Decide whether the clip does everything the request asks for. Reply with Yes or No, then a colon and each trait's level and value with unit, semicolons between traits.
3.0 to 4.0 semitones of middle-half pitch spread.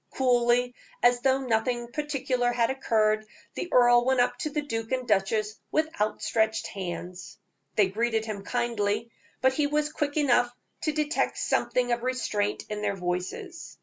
Yes: average, 3.4 semitones